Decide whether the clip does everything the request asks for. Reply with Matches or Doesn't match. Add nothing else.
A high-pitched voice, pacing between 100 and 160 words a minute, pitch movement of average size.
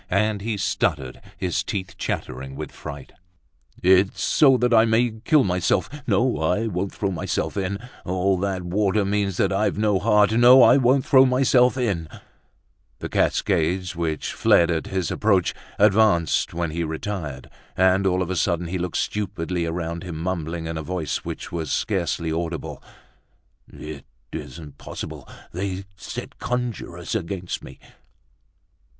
Doesn't match